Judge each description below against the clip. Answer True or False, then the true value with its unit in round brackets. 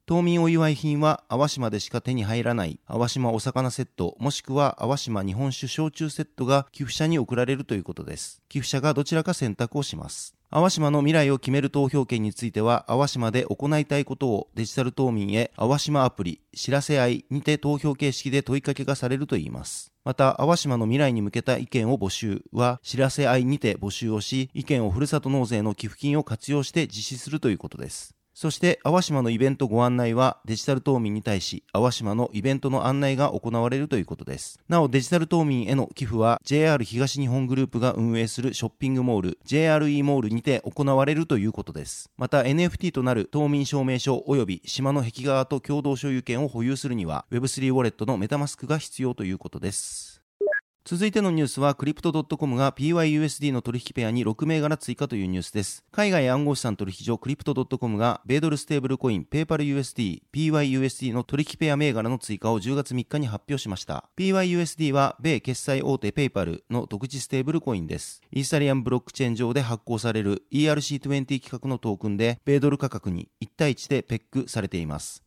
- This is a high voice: False (135 Hz)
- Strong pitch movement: False (3.6 semitones)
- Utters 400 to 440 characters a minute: True (425 characters per minute)